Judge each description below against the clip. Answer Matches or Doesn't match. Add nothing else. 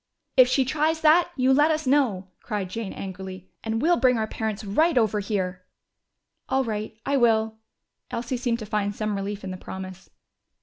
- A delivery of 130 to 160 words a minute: Doesn't match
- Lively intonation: Doesn't match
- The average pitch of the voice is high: Matches